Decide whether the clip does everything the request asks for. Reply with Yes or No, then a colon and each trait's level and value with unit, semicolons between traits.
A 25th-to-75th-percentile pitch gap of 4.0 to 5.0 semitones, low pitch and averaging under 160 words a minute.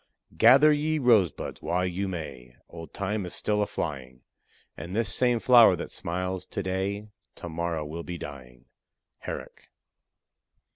Yes: average, 4.6 semitones; very low, 90 Hz; average, 145 wpm